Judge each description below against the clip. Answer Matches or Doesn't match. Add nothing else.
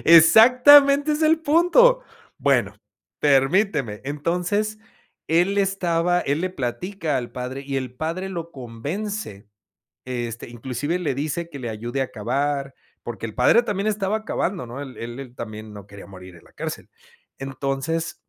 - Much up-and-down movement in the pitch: Matches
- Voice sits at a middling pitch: Matches